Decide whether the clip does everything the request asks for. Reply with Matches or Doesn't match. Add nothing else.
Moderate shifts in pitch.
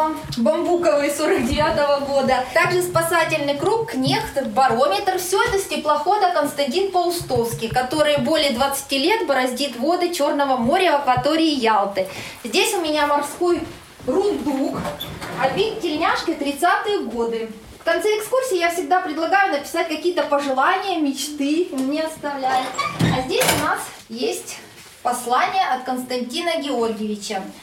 Matches